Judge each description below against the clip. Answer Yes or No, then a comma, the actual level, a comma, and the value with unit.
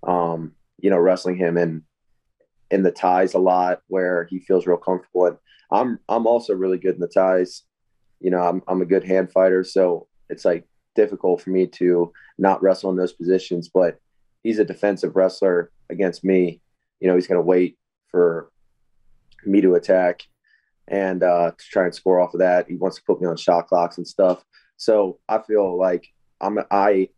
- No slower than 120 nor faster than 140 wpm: No, average, 190 wpm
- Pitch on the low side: Yes, very low, 90 Hz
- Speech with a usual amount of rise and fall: No, narrow, 1.0 semitones